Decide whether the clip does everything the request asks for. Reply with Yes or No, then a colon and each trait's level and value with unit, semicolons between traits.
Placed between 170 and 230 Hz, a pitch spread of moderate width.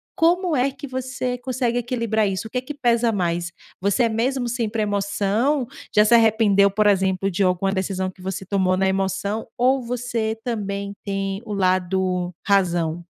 Yes: high, 205 Hz; average, 4.0 semitones